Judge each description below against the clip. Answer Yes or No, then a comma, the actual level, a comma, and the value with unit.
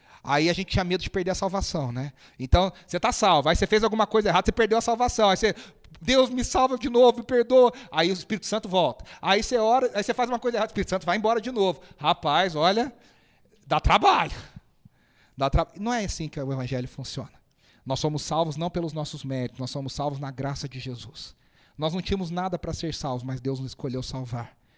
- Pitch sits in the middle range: Yes, medium, 175 Hz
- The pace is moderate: No, fast, 225 wpm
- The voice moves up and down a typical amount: No, wide, 8.0 semitones